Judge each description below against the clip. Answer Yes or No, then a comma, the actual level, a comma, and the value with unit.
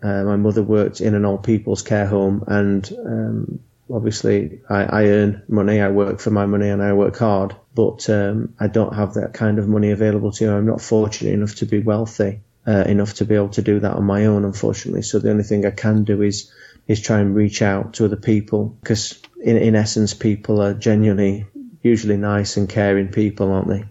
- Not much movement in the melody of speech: Yes, narrow, 1.3 semitones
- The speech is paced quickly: Yes, fast, 220 wpm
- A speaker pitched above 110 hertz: No, low, 105 Hz